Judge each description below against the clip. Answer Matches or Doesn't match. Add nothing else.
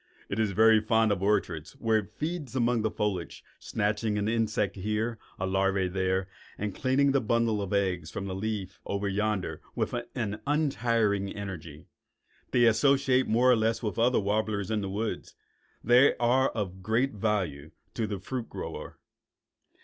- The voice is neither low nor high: Doesn't match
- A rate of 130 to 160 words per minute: Doesn't match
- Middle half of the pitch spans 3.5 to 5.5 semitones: Doesn't match